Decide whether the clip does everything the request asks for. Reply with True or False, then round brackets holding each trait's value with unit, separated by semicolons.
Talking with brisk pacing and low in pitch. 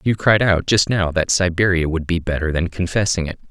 True (225 wpm; 90 Hz)